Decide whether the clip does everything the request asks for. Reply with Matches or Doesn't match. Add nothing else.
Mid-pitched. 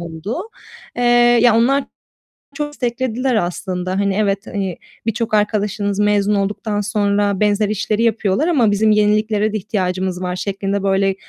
Doesn't match